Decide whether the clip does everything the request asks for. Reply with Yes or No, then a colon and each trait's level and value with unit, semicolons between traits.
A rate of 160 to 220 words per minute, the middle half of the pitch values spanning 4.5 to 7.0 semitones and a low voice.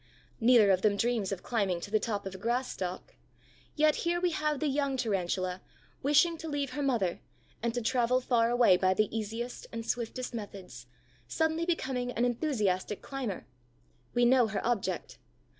No: average, 175 wpm; average, 4.8 semitones; high, 235 Hz